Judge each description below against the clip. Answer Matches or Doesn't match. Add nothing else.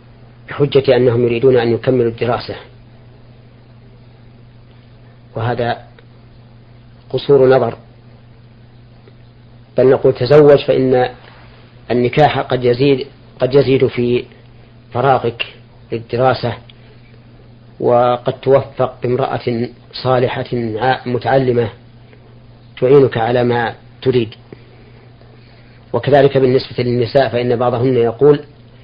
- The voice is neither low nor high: Doesn't match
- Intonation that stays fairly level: Matches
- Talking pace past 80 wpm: Doesn't match